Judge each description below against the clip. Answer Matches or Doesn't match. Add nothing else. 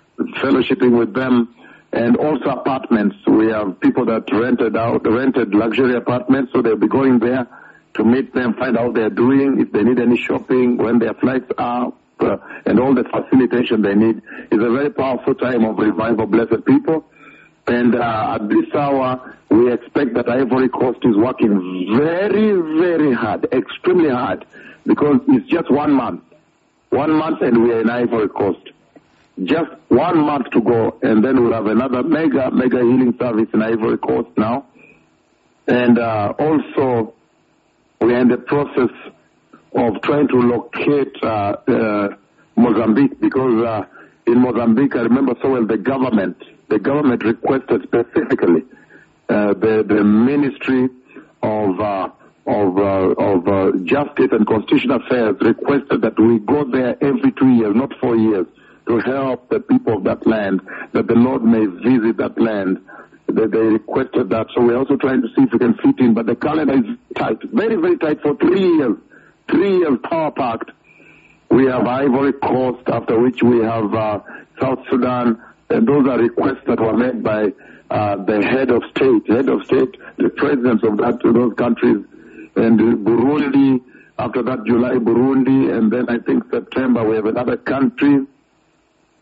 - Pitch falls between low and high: Doesn't match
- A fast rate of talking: Doesn't match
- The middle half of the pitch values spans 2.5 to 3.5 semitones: Matches